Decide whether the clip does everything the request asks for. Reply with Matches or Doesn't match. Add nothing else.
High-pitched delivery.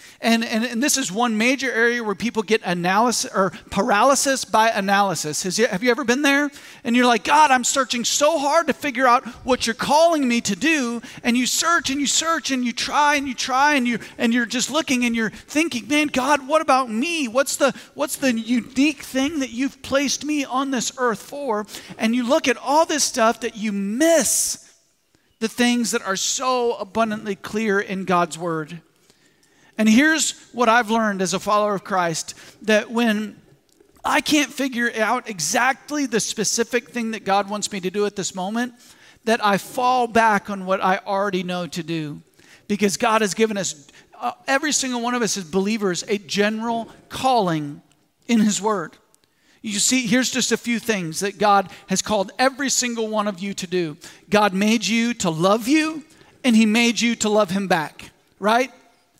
Matches